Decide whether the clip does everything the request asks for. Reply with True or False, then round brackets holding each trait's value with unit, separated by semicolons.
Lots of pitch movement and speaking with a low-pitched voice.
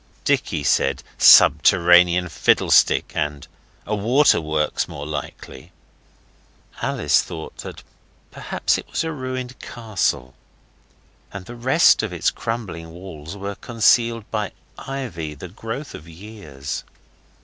True (6.8 semitones; 95 Hz)